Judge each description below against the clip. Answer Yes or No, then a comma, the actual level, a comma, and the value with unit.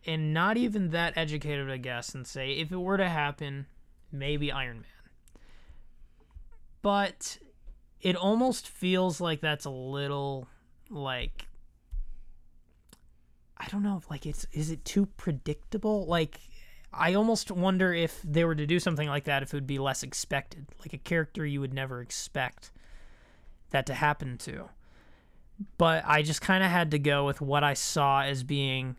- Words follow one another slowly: No, average, 160 wpm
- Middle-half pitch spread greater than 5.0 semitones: No, average, 4.7 semitones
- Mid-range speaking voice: Yes, medium, 150 Hz